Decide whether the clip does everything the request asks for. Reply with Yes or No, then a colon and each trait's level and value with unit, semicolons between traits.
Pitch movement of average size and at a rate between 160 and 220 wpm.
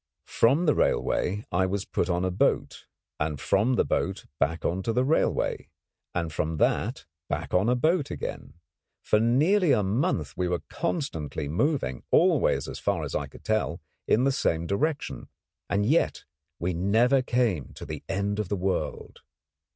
No: wide, 6.6 semitones; average, 165 wpm